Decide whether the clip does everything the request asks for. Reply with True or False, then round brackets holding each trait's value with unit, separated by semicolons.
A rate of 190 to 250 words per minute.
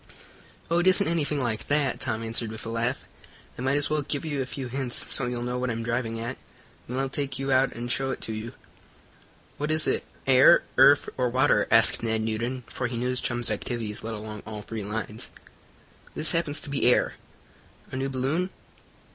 True (205 wpm)